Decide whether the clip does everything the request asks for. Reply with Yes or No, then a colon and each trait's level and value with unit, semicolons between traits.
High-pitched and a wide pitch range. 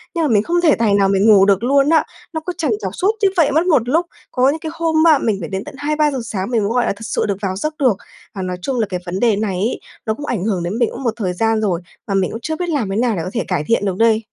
Yes: high, 225 Hz; wide, 6.9 semitones